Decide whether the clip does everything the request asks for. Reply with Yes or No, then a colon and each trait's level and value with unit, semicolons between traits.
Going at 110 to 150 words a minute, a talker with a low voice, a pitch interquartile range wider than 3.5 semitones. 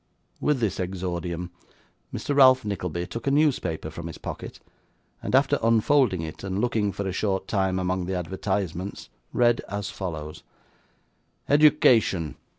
Yes: average, 140 wpm; very low, 95 Hz; average, 4.9 semitones